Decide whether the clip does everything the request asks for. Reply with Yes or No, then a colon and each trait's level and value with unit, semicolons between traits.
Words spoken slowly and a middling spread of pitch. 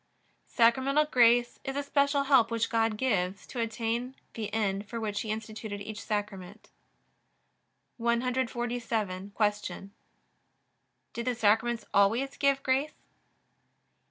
Yes: slow, 115 wpm; average, 3.2 semitones